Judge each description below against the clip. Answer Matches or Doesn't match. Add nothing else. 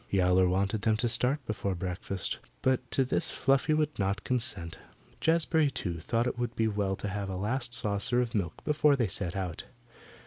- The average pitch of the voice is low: Matches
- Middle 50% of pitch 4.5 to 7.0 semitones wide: Matches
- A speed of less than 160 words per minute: Doesn't match